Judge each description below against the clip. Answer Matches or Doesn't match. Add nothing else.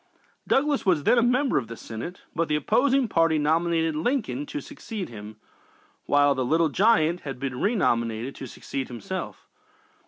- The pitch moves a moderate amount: Doesn't match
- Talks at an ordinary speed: Matches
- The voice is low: Doesn't match